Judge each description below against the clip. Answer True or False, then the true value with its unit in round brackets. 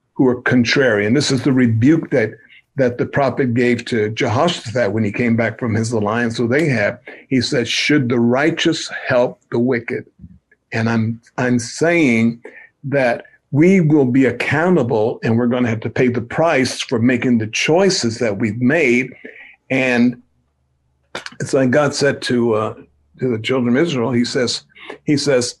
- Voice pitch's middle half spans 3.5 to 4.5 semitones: False (3.0 semitones)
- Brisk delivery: False (175 wpm)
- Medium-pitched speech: False (120 Hz)